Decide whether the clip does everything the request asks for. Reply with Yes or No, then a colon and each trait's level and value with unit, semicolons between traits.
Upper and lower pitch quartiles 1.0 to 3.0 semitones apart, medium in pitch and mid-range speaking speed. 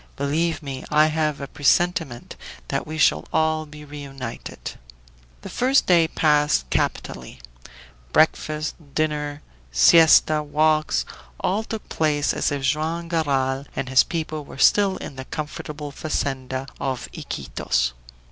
No: narrow, 2.5 semitones; medium, 150 Hz; slow, 130 wpm